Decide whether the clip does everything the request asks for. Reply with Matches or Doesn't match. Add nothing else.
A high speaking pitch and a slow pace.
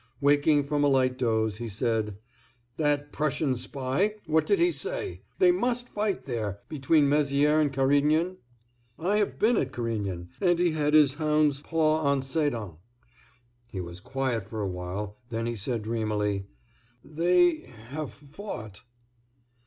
Doesn't match